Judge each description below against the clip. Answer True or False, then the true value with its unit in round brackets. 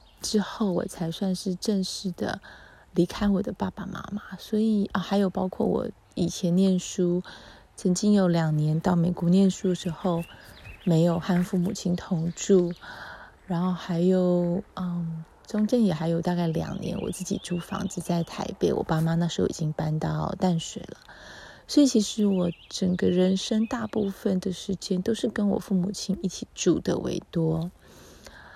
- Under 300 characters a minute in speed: True (240 characters per minute)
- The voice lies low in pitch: False (185 Hz)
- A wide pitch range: False (2.4 semitones)